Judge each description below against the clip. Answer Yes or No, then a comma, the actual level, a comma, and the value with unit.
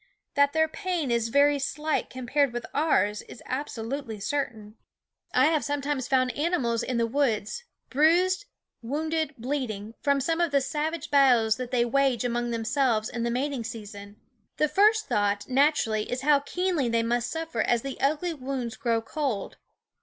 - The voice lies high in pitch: Yes, very high, 265 Hz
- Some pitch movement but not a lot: Yes, average, 4.2 semitones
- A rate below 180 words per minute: Yes, average, 160 wpm